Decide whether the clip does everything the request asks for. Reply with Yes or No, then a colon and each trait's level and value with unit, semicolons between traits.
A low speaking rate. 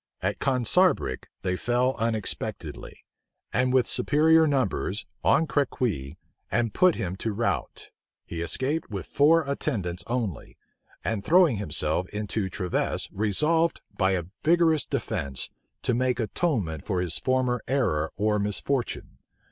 Yes: slow, 125 wpm